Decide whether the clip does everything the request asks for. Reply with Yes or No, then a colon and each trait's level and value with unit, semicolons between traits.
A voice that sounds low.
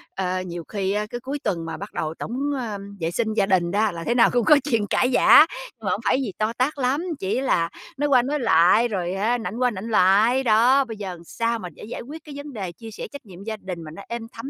No: high, 220 Hz